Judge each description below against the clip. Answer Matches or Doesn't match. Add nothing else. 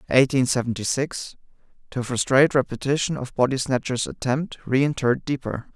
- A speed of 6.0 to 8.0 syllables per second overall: Doesn't match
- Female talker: Doesn't match